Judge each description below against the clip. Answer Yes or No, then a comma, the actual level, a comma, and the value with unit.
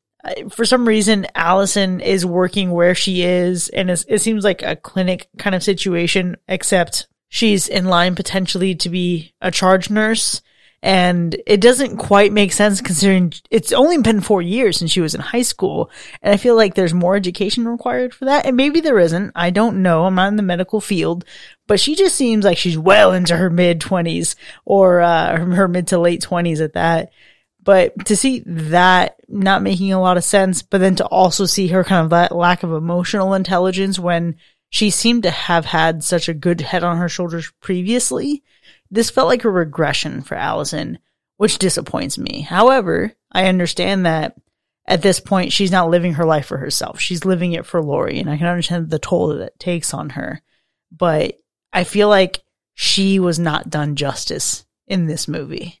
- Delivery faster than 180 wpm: Yes, average, 190 wpm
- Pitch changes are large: No, average, 2.7 semitones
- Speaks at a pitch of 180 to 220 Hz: Yes, medium, 185 Hz